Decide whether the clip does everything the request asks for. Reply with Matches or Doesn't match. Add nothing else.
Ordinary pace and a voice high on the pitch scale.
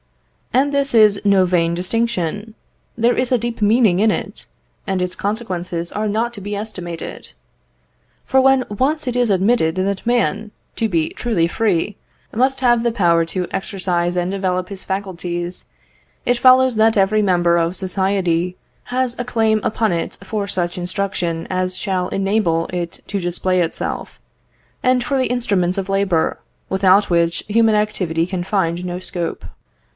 Matches